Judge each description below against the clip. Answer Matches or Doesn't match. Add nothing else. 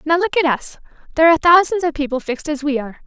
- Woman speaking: Matches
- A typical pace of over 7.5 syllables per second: Matches